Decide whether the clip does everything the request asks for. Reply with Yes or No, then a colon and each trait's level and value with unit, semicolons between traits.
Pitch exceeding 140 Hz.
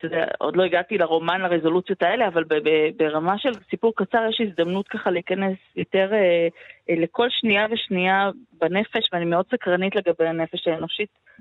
Yes: medium, 185 Hz